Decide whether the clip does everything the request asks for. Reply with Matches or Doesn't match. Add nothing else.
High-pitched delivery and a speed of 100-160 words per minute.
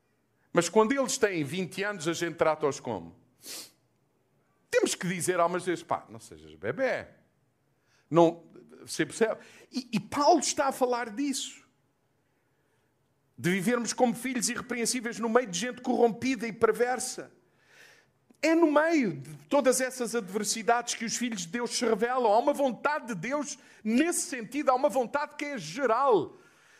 Matches